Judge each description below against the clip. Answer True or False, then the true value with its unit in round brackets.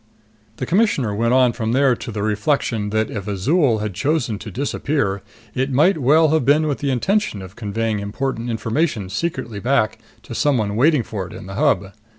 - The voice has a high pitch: False (120 Hz)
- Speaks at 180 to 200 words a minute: True (185 wpm)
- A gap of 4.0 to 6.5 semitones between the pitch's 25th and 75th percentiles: True (5.3 semitones)